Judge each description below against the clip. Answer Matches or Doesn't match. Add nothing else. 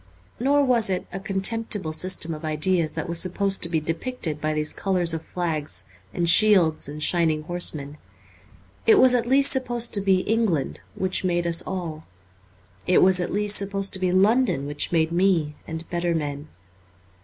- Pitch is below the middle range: Doesn't match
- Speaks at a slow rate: Doesn't match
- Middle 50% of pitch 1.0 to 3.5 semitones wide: Doesn't match